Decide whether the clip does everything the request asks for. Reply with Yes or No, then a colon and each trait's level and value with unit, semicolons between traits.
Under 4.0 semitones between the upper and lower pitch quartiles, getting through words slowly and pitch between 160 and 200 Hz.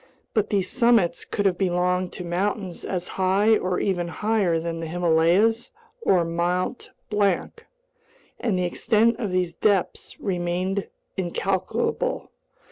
Yes: average, 2.8 semitones; slow, 125 wpm; medium, 185 Hz